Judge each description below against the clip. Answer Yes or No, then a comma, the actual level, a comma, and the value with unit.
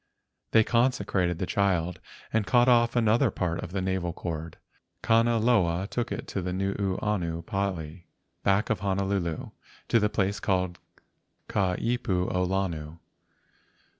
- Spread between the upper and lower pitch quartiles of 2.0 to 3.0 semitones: No, average, 3.4 semitones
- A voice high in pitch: No, very low, 95 Hz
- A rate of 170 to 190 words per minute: No, slow, 135 wpm